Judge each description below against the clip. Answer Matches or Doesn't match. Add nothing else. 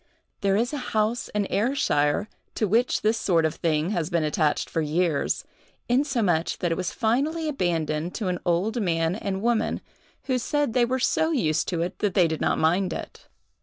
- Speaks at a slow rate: Doesn't match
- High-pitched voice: Matches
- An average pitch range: Doesn't match